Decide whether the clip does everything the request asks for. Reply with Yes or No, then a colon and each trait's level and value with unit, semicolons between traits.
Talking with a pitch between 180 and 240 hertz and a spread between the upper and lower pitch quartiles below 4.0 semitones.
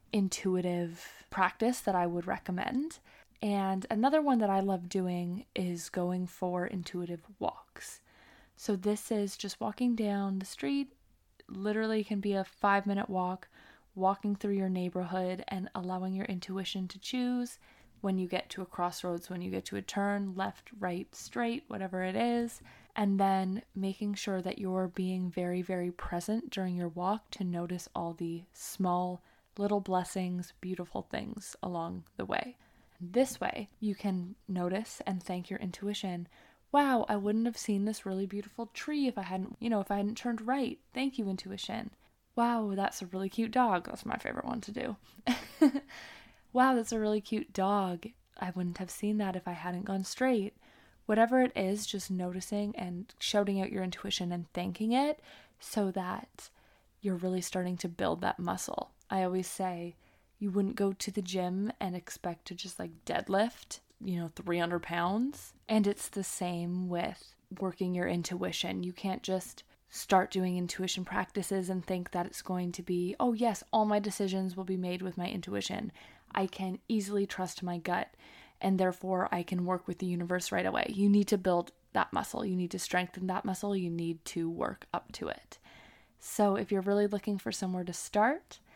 Yes: high, 190 Hz; narrow, 2.5 semitones